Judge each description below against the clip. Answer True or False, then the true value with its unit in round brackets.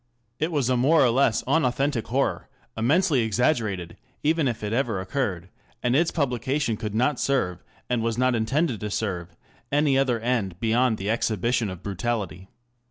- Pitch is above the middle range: False (120 Hz)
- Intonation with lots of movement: False (4.4 semitones)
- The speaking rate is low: False (165 wpm)